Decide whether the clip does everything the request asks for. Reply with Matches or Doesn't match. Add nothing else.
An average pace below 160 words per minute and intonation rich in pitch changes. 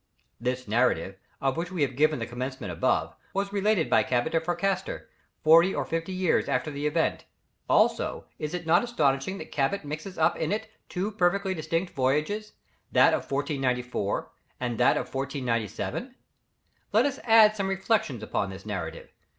Doesn't match